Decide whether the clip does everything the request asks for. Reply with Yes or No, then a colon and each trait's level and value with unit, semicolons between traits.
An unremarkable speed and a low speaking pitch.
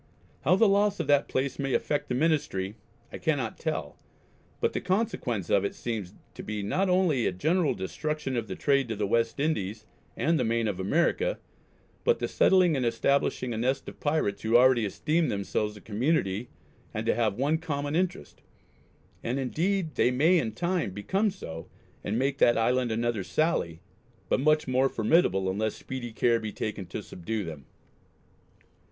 Yes: average, 175 wpm; low, 125 Hz